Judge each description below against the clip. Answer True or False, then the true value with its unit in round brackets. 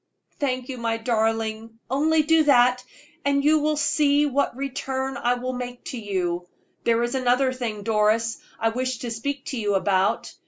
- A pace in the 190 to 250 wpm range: False (170 wpm)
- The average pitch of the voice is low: False (245 Hz)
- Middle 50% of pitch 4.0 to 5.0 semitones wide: False (3.5 semitones)